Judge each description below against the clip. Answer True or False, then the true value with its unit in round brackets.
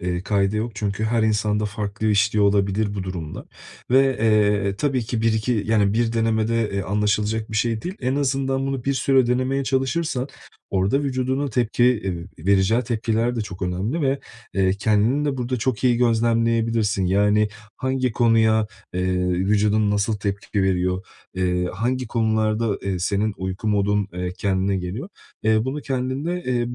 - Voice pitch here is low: True (110 Hz)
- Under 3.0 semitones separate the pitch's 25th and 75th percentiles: False (3.6 semitones)